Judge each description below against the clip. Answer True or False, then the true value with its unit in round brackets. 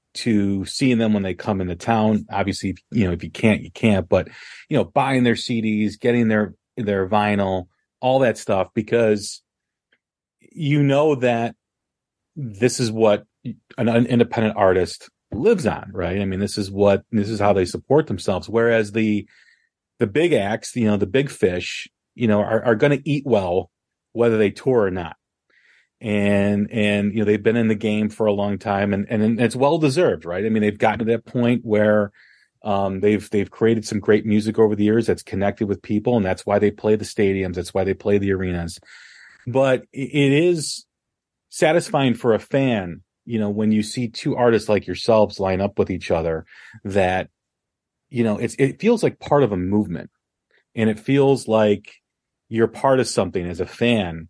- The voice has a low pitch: True (110 Hz)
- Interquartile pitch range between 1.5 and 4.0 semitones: True (2.9 semitones)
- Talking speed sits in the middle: True (190 wpm)